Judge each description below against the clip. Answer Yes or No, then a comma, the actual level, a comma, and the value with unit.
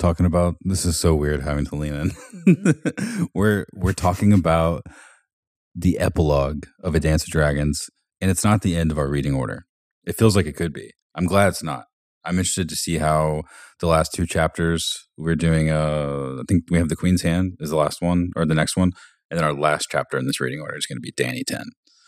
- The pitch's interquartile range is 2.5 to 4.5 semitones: Yes, average, 3.2 semitones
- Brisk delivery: Yes, fast, 225 wpm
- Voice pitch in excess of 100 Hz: No, very low, 85 Hz